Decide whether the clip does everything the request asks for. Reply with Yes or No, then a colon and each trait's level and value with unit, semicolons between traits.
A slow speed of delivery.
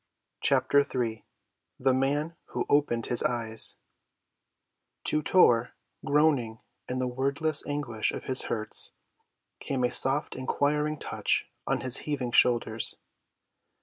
Yes: slow, 115 wpm